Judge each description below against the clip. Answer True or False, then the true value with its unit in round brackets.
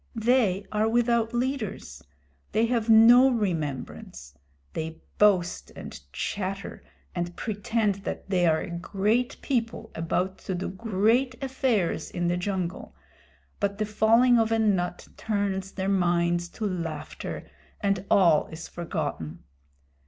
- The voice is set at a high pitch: True (195 Hz)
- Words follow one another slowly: True (130 wpm)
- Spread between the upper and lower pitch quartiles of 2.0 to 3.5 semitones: False (4.4 semitones)